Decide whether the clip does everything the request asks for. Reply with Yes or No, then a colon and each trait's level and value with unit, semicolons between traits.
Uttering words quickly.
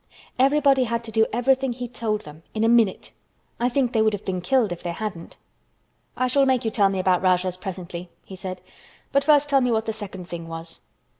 Yes: fast, 215 wpm